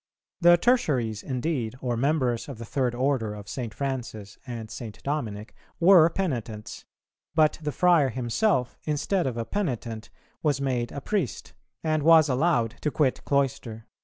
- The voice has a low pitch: Yes, low, 130 Hz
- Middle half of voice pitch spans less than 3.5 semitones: No, average, 5.1 semitones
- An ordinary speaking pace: Yes, average, 150 wpm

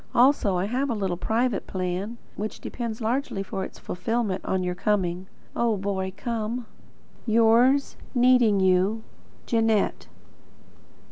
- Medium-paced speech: No, slow, 125 wpm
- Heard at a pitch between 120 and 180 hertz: No, high, 215 Hz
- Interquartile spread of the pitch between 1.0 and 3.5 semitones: No, average, 3.9 semitones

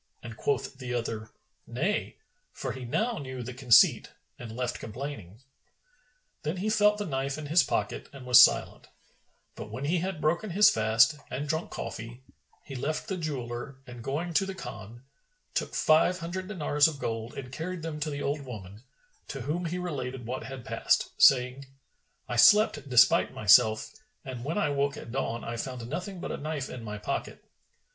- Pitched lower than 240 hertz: Yes, low, 135 Hz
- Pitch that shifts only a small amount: No, average, 4.8 semitones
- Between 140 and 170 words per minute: No, average, 180 wpm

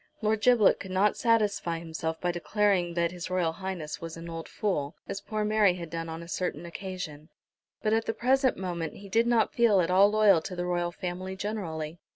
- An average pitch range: Yes, average, 3.8 semitones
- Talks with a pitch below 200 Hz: Yes, medium, 185 Hz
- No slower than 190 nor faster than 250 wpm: Yes, average, 195 wpm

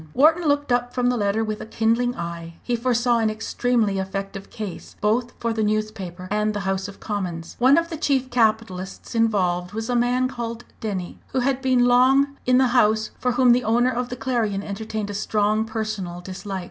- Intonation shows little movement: No, average, 3.5 semitones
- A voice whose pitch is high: Yes, high, 225 Hz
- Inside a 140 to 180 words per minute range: No, average, 200 wpm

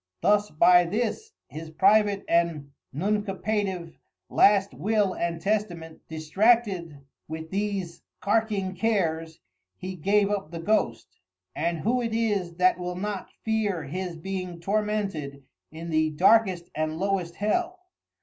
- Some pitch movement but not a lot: Yes, average, 4.0 semitones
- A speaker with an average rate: No, slow, 125 wpm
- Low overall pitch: No, medium, 185 Hz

